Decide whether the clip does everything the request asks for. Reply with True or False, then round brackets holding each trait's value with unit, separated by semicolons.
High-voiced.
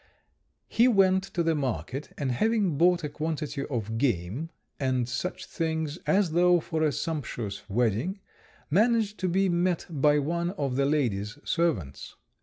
False (155 Hz)